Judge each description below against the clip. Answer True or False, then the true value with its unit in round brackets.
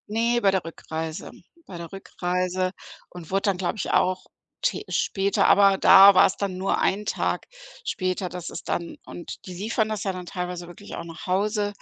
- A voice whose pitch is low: False (185 Hz)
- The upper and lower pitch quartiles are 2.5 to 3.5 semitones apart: False (2.1 semitones)